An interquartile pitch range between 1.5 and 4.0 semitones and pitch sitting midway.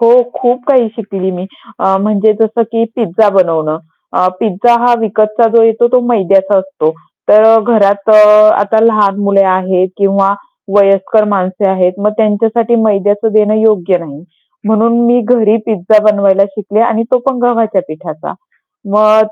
No: narrow, 2.6 semitones; high, 210 Hz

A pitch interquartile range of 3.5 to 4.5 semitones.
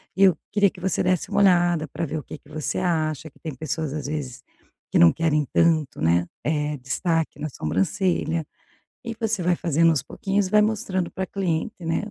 Yes: average, 3.8 semitones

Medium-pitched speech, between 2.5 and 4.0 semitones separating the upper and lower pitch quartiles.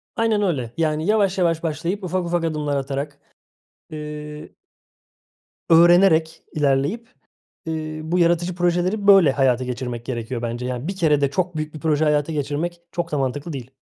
Yes: medium, 155 Hz; average, 3.6 semitones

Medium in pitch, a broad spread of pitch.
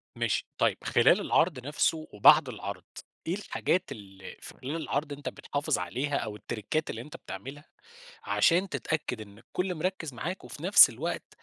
Yes: medium, 145 Hz; wide, 6.5 semitones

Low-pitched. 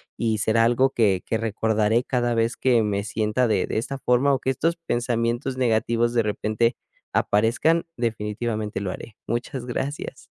Yes: low, 115 Hz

